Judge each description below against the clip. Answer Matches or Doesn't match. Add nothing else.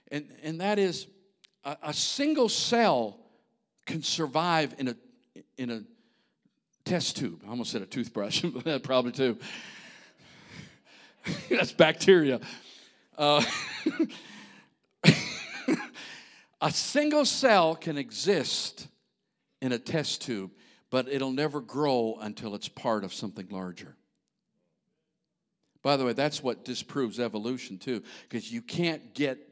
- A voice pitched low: Doesn't match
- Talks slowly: Matches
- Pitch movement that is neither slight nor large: Doesn't match